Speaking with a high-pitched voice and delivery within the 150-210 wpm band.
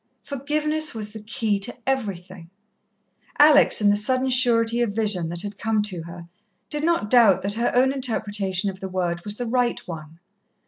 Yes: high, 215 Hz; average, 180 wpm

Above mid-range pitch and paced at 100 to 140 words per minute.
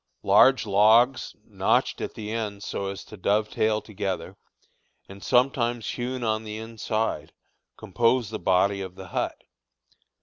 No: low, 110 Hz; slow, 135 wpm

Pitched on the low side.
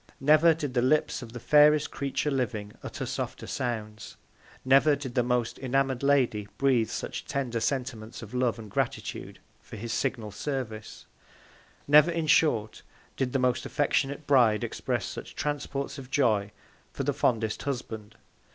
Yes: low, 130 Hz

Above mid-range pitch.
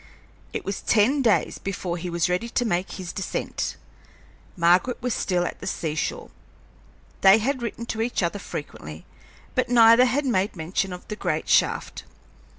Yes: high, 195 Hz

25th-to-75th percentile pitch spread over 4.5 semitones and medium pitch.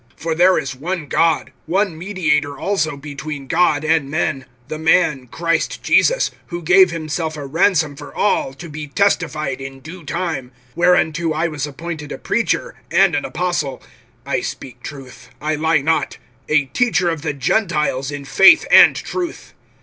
No: average, 3.3 semitones; medium, 155 Hz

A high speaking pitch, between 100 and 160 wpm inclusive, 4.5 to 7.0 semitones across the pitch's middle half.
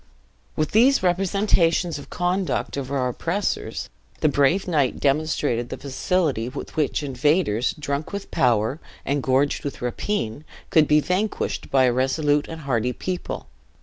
No: medium, 145 Hz; average, 150 wpm; average, 5.2 semitones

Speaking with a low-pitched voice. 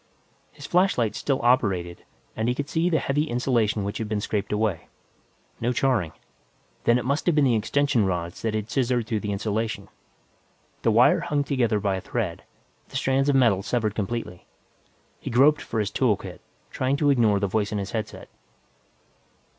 Yes: low, 115 Hz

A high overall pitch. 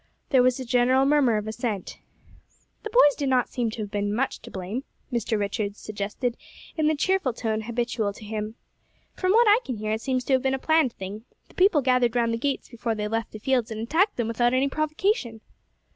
Yes: high, 240 Hz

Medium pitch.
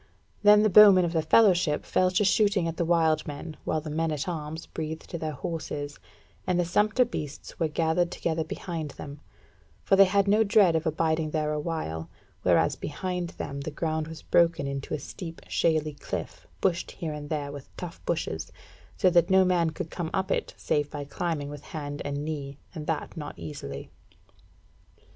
Yes: medium, 160 Hz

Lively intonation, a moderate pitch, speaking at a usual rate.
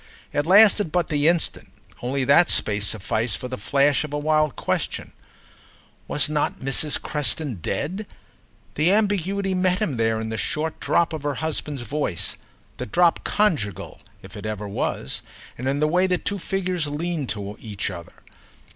Yes: wide, 6.2 semitones; medium, 150 Hz; average, 165 wpm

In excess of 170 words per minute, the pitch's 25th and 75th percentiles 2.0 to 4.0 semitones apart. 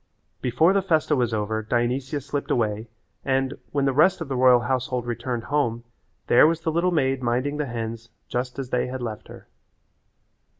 Yes: average, 180 wpm; average, 3.3 semitones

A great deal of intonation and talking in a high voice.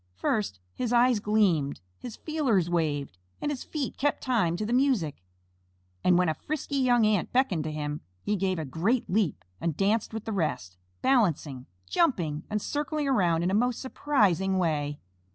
Yes: wide, 7.6 semitones; high, 200 Hz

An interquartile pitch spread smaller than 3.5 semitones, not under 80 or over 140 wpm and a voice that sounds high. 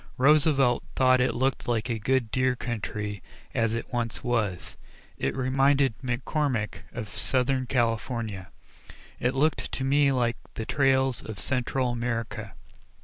No: average, 2.8 semitones; slow, 135 wpm; low, 125 Hz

